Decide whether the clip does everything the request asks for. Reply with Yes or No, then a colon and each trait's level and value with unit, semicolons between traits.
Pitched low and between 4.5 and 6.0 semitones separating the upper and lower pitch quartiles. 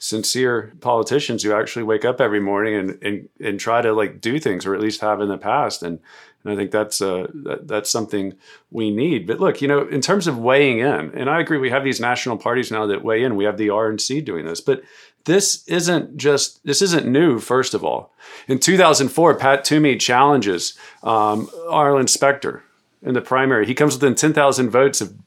Yes: low, 125 Hz; average, 5.0 semitones